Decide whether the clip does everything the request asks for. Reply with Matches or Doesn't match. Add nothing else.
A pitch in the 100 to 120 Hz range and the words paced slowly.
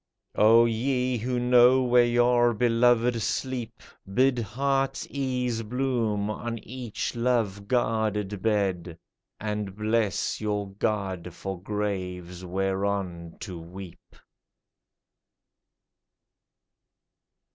Matches